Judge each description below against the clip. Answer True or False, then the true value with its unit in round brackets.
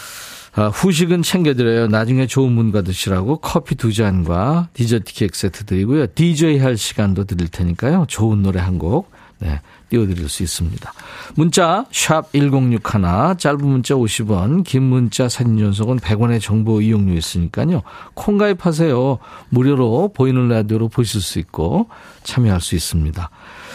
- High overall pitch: False (115 Hz)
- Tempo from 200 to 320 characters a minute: True (300 characters per minute)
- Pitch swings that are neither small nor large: False (6.1 semitones)